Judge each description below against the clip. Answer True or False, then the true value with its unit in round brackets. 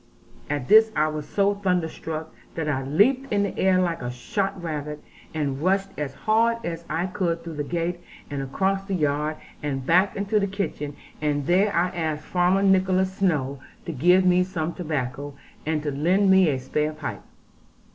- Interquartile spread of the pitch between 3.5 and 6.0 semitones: True (4.2 semitones)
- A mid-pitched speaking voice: True (170 Hz)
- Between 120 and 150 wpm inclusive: False (180 wpm)